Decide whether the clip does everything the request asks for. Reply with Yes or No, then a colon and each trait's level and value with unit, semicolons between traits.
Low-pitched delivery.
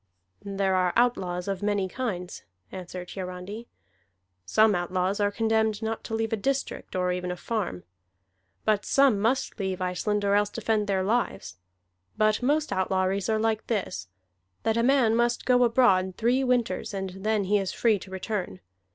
No: high, 205 Hz